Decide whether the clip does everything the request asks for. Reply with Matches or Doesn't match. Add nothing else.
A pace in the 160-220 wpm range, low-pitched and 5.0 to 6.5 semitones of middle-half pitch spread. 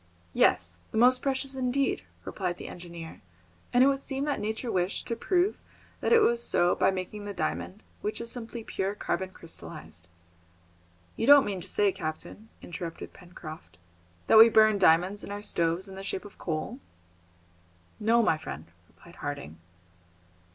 Doesn't match